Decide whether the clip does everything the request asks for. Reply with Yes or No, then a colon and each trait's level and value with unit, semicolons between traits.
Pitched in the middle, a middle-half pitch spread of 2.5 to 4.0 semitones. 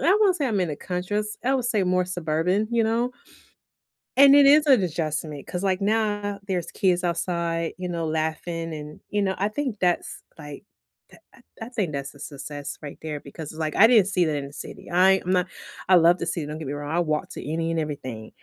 No: medium, 175 Hz; average, 4.9 semitones